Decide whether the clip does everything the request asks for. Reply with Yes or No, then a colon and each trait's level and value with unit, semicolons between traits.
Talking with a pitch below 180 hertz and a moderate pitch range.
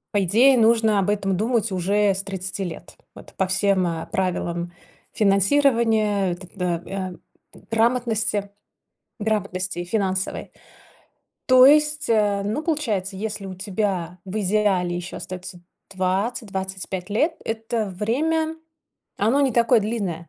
No: high, 200 Hz; average, 3.2 semitones